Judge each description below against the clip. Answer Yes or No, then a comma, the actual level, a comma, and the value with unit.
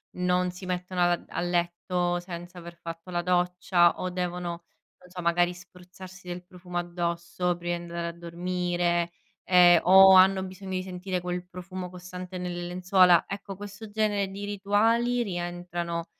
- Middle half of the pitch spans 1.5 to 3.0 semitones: No, narrow, 1.0 semitones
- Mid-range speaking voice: Yes, medium, 180 Hz